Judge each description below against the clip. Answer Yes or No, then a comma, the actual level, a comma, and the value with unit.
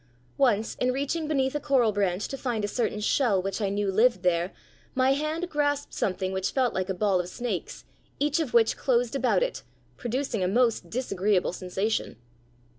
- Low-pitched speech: No, high, 230 Hz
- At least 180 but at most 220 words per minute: Yes, average, 185 wpm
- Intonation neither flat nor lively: No, wide, 5.7 semitones